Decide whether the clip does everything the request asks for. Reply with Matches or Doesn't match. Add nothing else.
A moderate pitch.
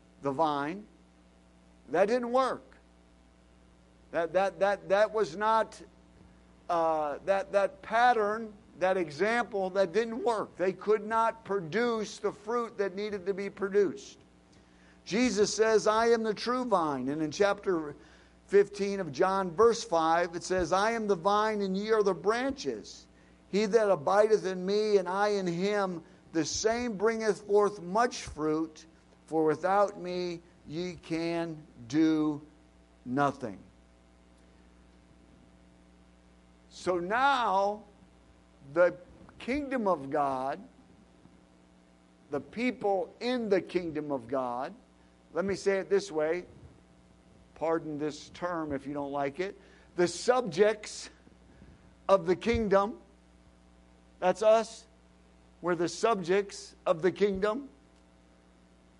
Matches